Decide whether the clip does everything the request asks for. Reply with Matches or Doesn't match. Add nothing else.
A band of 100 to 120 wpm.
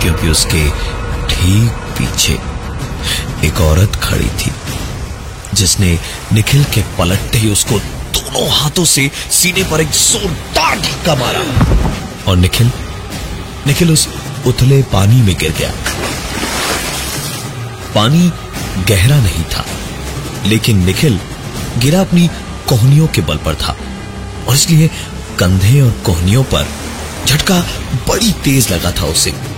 Matches